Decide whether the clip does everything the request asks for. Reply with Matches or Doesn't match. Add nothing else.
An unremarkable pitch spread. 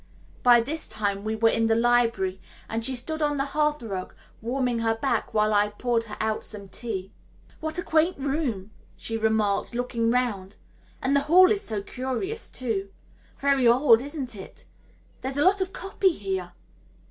Matches